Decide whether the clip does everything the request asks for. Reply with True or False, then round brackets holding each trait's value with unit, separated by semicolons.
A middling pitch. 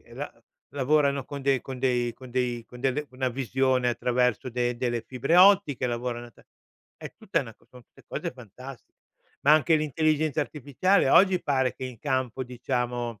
False (130 Hz)